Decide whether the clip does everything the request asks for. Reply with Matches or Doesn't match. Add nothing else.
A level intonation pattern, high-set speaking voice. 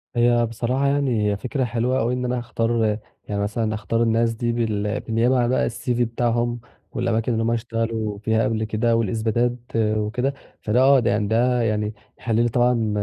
Doesn't match